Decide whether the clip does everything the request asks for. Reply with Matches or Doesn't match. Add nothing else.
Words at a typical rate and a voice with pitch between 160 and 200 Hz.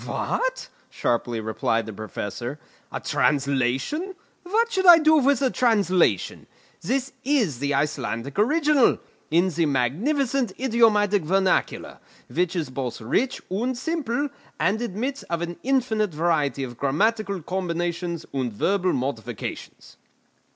Doesn't match